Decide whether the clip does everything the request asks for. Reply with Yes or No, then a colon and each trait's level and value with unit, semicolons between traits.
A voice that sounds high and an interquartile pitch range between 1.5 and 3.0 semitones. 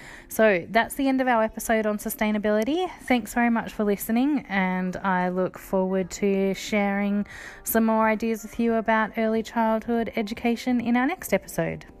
Yes: high, 220 Hz; average, 2.7 semitones